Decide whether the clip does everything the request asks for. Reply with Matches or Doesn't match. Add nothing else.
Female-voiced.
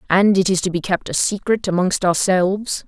Matches